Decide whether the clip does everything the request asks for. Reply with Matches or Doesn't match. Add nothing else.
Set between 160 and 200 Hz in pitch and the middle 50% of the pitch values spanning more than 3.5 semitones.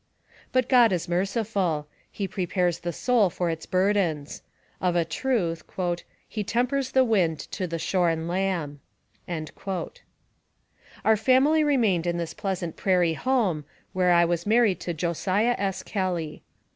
Matches